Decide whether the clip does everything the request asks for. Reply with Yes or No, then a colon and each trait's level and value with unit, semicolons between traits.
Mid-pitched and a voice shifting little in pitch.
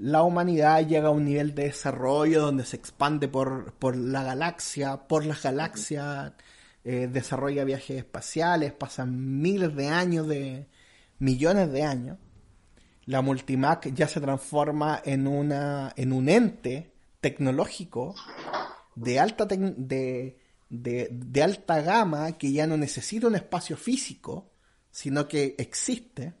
No: medium, 145 Hz; average, 3.2 semitones